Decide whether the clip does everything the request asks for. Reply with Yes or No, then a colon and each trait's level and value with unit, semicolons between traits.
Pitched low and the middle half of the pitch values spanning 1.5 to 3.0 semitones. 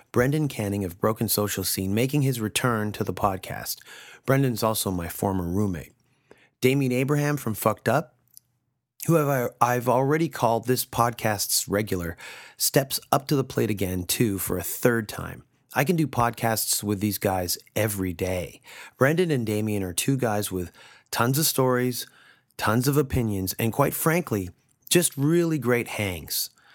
No: low, 115 Hz; average, 4.6 semitones